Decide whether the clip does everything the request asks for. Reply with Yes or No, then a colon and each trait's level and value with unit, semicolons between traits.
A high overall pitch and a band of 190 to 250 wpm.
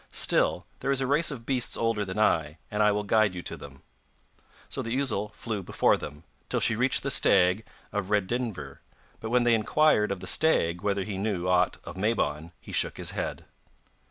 No: low, 105 Hz; average, 200 wpm